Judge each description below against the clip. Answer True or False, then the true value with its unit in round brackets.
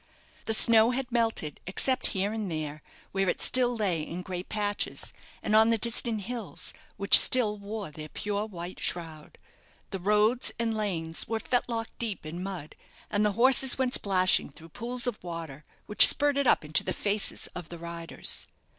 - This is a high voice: True (205 Hz)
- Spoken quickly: False (170 wpm)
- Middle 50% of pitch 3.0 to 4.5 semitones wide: False (5.0 semitones)